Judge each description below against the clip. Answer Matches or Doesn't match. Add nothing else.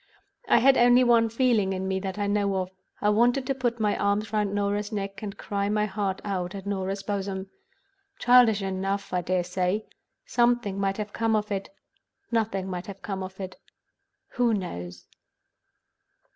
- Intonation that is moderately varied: Doesn't match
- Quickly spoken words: Doesn't match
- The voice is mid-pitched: Doesn't match